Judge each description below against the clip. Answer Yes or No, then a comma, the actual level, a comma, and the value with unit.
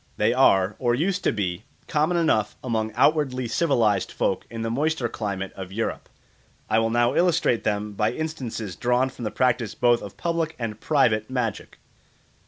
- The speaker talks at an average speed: Yes, average, 170 wpm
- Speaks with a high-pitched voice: No, low, 120 Hz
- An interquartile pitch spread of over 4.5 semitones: Yes, average, 5.0 semitones